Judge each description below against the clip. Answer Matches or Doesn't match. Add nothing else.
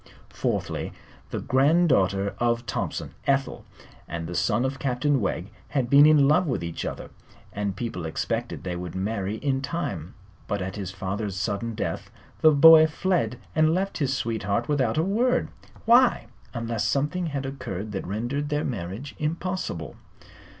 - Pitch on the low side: Matches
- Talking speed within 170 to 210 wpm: Doesn't match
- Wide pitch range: Matches